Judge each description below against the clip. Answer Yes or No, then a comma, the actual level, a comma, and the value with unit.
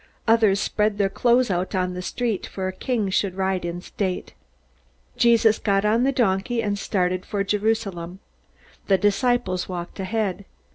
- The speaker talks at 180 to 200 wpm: No, average, 155 wpm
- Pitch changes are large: No, average, 3.1 semitones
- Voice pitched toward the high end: Yes, high, 200 Hz